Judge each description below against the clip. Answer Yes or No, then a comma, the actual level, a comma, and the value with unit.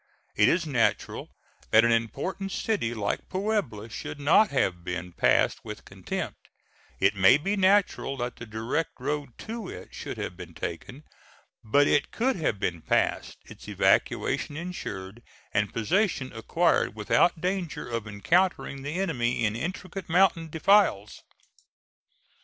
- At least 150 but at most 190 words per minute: No, average, 140 wpm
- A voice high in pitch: No, medium, 140 Hz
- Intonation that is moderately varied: No, wide, 9.0 semitones